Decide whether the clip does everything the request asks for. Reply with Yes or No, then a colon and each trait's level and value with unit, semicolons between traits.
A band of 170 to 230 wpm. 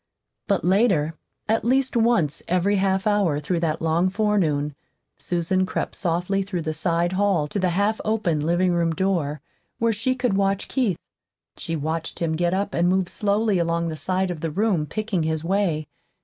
Yes: average, 175 wpm